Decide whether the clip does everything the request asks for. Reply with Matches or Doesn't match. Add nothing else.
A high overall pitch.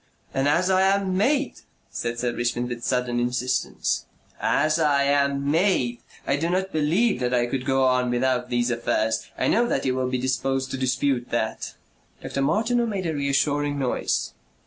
Doesn't match